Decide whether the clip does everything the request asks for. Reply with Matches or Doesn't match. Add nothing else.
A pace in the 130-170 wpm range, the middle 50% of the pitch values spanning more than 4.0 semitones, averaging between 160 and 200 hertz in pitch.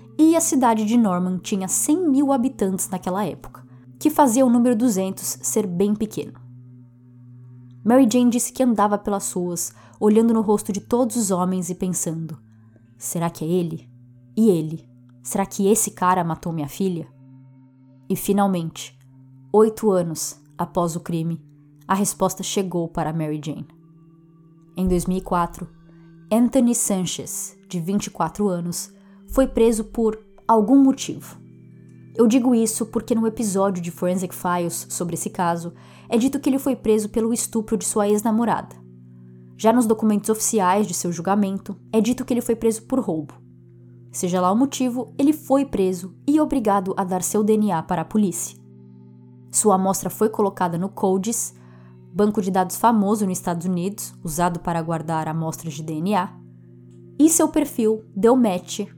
Matches